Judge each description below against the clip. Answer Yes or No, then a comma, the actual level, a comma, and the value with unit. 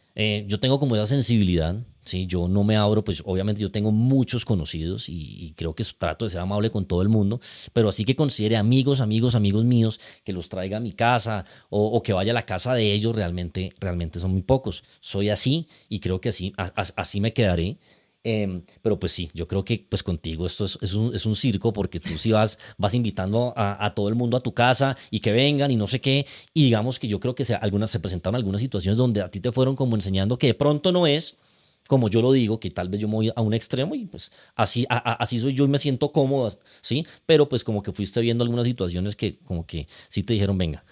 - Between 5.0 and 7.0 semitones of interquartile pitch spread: No, average, 3.8 semitones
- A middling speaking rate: No, fast, 250 wpm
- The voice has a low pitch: Yes, low, 110 Hz